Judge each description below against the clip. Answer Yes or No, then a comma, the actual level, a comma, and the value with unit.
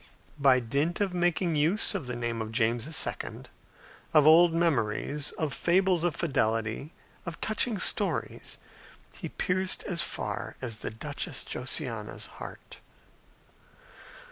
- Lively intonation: Yes, wide, 6.4 semitones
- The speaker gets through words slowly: Yes, slow, 125 wpm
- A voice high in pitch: No, medium, 155 Hz